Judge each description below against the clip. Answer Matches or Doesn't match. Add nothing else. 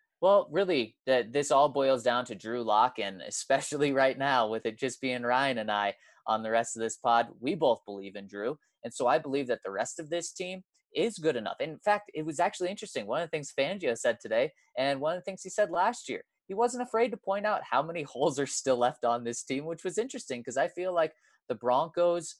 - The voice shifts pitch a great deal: Matches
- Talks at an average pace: Doesn't match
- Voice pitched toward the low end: Doesn't match